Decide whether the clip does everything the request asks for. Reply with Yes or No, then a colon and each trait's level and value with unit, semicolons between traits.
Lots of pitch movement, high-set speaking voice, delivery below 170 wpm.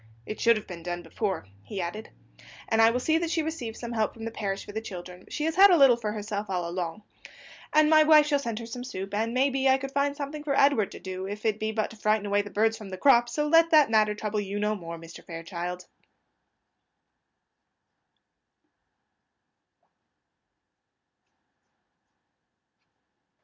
No: wide, 5.7 semitones; high, 220 Hz; average, 185 wpm